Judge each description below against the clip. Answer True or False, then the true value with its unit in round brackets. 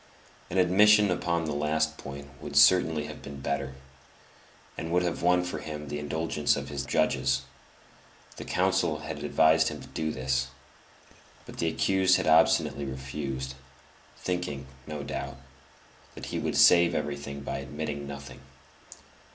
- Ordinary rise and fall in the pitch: True (3.0 semitones)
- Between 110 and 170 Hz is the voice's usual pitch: False (75 Hz)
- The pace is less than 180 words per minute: True (145 wpm)